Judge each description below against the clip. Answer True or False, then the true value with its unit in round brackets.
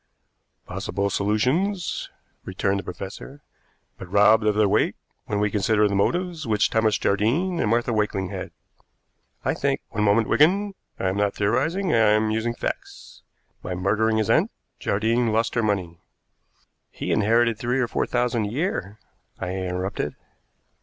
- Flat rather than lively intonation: False (3.1 semitones)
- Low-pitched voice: True (110 Hz)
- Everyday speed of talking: True (160 wpm)